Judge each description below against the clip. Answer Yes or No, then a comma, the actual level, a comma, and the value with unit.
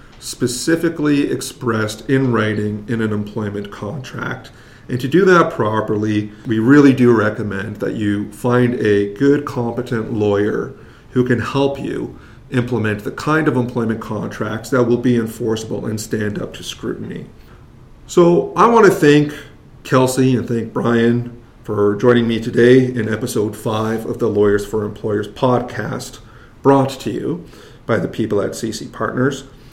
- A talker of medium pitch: No, low, 120 Hz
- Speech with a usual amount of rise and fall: Yes, average, 3.3 semitones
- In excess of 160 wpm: No, average, 150 wpm